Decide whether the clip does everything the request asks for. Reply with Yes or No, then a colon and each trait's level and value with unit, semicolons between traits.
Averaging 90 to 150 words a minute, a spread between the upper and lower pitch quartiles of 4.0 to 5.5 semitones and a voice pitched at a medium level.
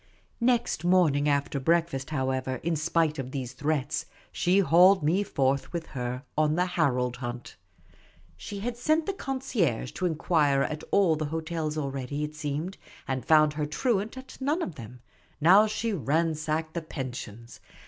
No: average, 160 wpm; average, 4.8 semitones; medium, 155 Hz